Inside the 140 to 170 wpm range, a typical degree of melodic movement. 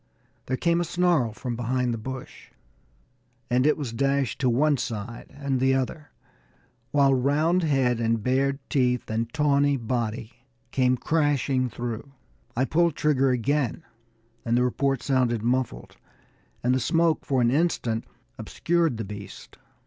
Yes: average, 145 wpm; average, 3.2 semitones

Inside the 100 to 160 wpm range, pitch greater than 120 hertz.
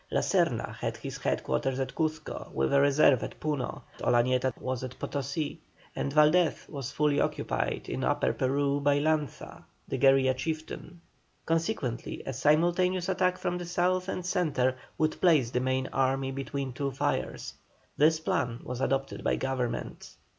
Yes: average, 155 wpm; medium, 140 Hz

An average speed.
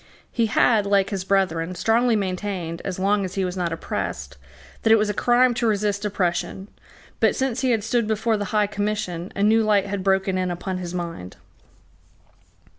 Yes: average, 190 wpm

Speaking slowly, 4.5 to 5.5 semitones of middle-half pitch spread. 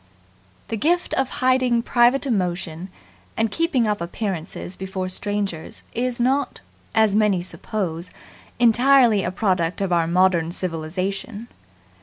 Yes: slow, 120 wpm; average, 4.8 semitones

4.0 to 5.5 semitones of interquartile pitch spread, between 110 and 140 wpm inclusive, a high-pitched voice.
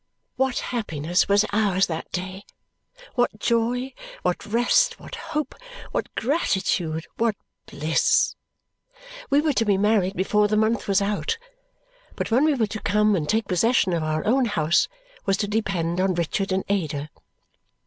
No: average, 4.3 semitones; average, 155 wpm; high, 205 Hz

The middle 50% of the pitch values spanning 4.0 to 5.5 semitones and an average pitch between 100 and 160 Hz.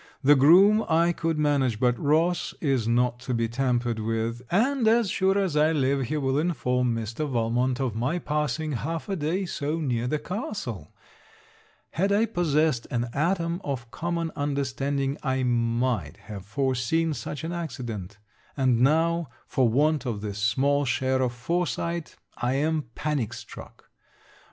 Yes: average, 5.1 semitones; medium, 140 Hz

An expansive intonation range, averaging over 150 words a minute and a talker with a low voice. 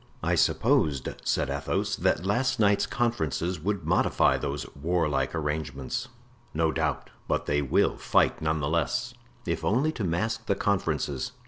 No: wide, 5.8 semitones; average, 145 wpm; very low, 85 Hz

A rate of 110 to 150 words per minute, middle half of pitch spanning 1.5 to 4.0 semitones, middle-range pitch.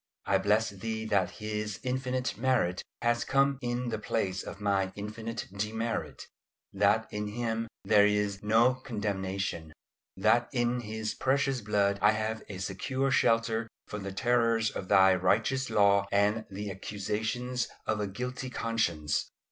No: average, 145 wpm; average, 2.9 semitones; low, 110 Hz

